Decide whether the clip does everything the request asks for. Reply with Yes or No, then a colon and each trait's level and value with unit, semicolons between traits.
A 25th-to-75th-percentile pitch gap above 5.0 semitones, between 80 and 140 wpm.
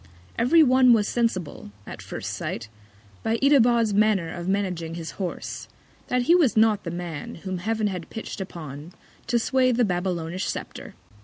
No: wide, 5.4 semitones; average, 160 wpm